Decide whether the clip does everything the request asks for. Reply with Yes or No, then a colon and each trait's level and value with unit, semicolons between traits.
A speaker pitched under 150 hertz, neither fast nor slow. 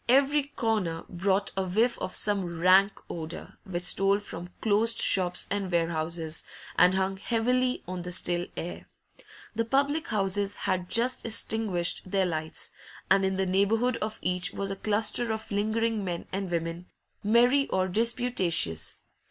No: high, 195 Hz; average, 150 wpm